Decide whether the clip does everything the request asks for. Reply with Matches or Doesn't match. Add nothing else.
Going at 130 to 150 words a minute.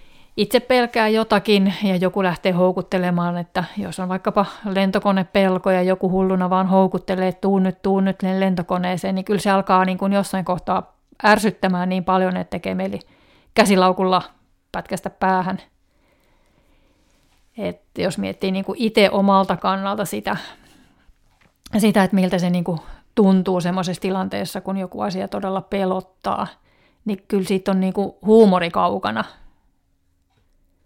Matches